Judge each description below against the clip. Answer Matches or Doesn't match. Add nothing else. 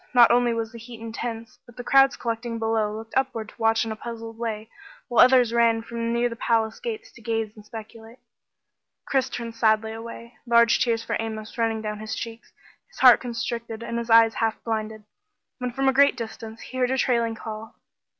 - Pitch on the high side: Matches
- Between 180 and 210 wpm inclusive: Matches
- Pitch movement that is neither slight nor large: Doesn't match